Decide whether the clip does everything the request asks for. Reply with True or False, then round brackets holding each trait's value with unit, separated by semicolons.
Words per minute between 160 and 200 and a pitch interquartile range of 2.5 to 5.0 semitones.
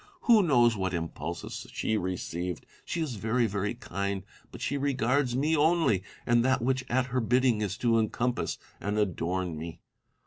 False (170 wpm; 5.4 semitones)